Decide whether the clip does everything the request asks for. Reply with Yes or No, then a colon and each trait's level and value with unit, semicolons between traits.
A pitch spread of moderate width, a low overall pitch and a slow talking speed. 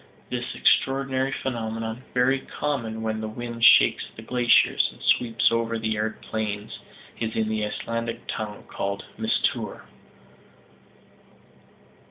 No: narrow, 2.0 semitones; low, 115 Hz; slow, 120 wpm